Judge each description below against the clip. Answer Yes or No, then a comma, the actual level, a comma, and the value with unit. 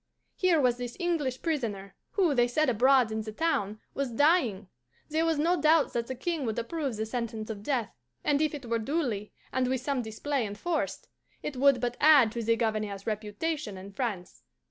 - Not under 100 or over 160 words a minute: No, average, 190 wpm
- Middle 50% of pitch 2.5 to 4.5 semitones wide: No, average, 5.3 semitones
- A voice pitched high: Yes, very high, 250 Hz